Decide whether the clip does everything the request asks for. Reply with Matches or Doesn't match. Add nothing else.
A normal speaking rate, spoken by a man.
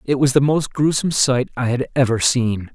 Doesn't match